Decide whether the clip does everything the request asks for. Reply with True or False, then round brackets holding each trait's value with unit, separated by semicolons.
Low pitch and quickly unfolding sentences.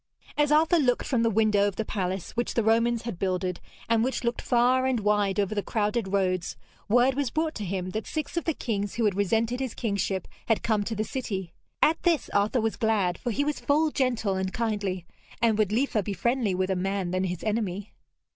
False (215 Hz; 220 wpm)